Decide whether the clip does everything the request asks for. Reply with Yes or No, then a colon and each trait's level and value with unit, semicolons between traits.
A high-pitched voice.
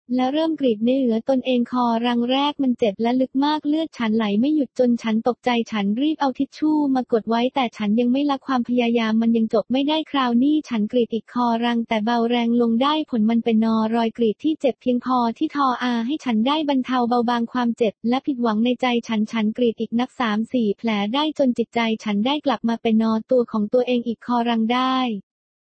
Yes: high, 245 Hz